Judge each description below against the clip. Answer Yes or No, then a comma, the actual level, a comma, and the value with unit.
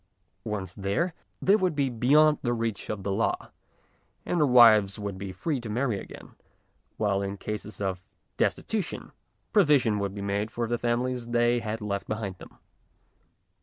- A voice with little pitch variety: No, average, 4.0 semitones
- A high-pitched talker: No, low, 115 Hz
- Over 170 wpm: No, average, 165 wpm